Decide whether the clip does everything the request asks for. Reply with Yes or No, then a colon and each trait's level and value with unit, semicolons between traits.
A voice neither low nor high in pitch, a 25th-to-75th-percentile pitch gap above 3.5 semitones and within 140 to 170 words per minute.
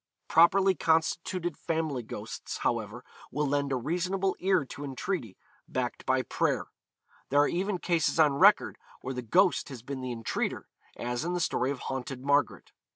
Yes: medium, 145 Hz; average, 5.3 semitones; average, 160 wpm